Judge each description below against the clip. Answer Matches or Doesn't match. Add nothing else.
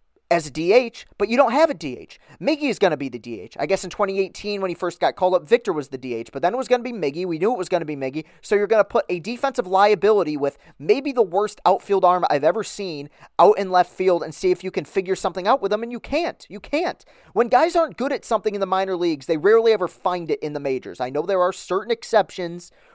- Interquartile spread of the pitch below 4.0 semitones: Doesn't match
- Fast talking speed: Matches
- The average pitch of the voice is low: Doesn't match